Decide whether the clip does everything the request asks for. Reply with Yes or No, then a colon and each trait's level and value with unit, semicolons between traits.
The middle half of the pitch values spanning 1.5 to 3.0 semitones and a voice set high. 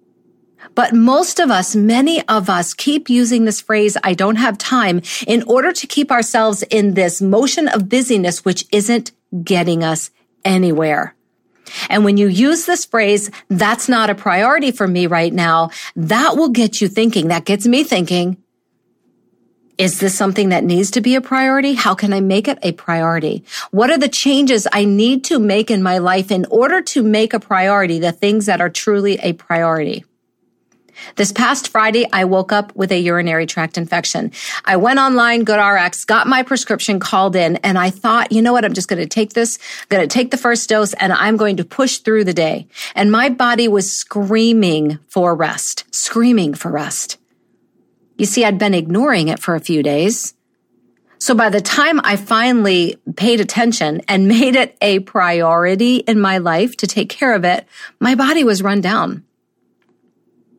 No: average, 4.5 semitones; high, 210 Hz